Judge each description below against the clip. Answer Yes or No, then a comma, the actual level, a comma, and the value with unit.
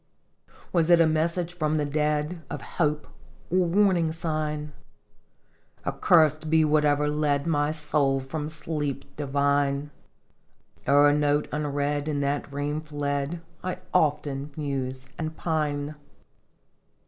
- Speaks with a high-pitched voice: No, medium, 150 Hz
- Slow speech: Yes, slow, 115 wpm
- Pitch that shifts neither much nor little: No, narrow, 1.6 semitones